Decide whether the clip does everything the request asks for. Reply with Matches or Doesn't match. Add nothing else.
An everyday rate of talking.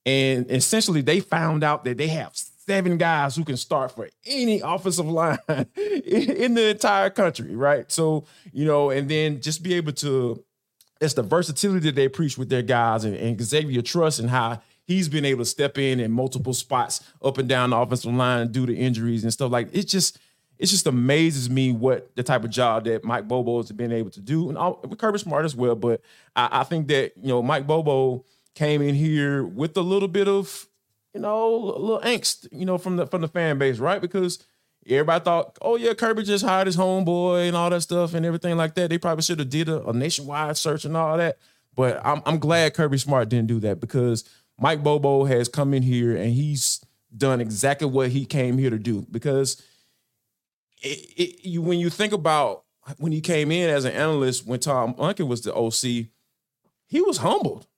Doesn't match